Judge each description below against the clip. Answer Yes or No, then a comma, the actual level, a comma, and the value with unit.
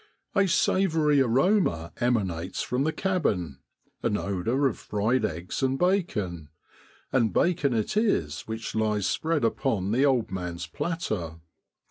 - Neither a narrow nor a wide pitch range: No, wide, 8.8 semitones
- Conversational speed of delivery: No, slow, 130 wpm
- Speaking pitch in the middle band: No, low, 115 Hz